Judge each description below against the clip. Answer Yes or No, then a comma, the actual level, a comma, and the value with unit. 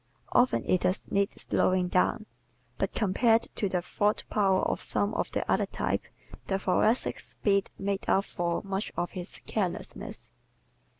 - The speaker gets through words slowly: No, average, 155 wpm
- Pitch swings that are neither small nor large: No, narrow, 2.2 semitones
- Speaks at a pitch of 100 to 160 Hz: No, high, 195 Hz